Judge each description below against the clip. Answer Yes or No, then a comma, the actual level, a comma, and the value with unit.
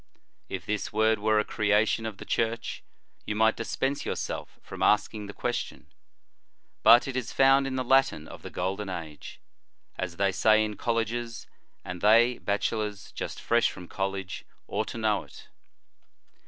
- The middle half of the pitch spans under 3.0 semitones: Yes, narrow, 2.5 semitones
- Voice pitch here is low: Yes, low, 110 Hz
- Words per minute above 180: No, average, 160 wpm